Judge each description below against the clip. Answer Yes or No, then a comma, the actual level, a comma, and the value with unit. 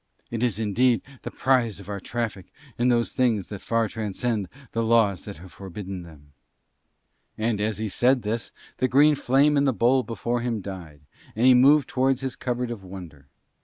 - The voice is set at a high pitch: No, low, 115 Hz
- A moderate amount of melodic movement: Yes, average, 4.0 semitones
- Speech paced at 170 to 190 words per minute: Yes, average, 185 wpm